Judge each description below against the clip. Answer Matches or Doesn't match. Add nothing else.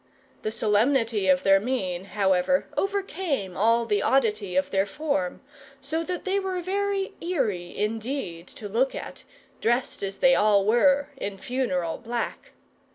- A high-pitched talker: Matches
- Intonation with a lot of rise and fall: Matches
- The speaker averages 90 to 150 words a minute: Matches